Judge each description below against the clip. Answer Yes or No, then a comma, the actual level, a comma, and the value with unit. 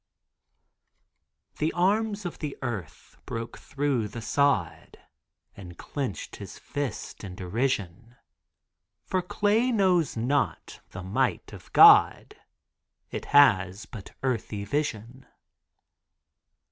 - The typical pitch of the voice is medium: No, low, 130 Hz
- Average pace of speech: No, slow, 100 wpm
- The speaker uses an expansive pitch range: Yes, wide, 6.6 semitones